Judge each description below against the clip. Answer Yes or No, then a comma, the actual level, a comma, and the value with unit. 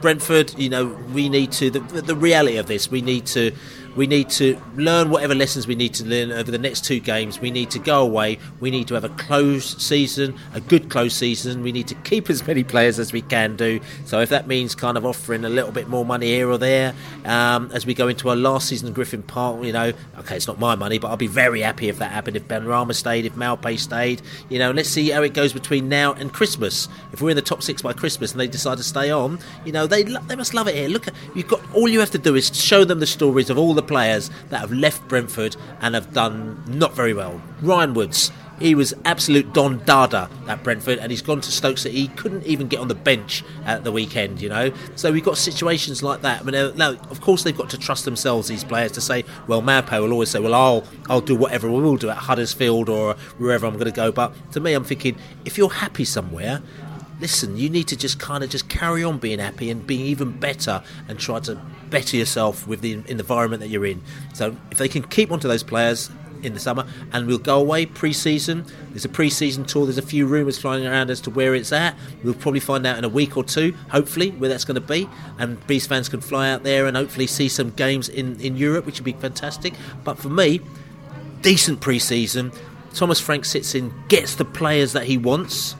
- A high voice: No, low, 135 Hz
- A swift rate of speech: Yes, fast, 245 wpm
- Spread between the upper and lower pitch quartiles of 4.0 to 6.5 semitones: No, average, 3.6 semitones